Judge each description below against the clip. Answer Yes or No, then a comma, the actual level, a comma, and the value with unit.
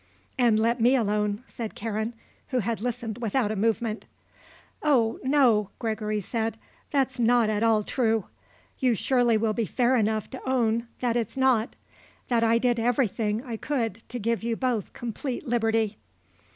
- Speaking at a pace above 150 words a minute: Yes, average, 160 wpm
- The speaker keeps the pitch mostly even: Yes, narrow, 2.1 semitones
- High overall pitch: Yes, high, 230 Hz